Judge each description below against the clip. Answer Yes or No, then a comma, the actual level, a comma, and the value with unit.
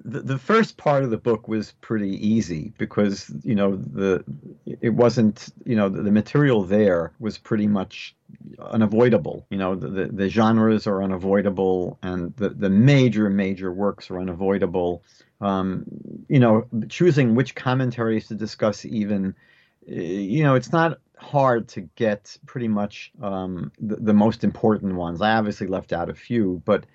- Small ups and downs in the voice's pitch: No, average, 3.3 semitones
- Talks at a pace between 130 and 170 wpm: Yes, average, 165 wpm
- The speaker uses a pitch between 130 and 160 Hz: No, low, 105 Hz